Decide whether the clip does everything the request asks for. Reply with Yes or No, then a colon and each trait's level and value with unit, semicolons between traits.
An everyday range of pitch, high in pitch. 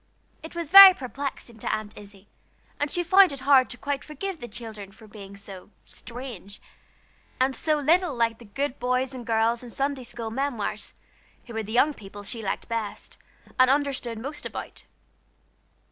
Yes: average, 4.4 semitones; high, 245 Hz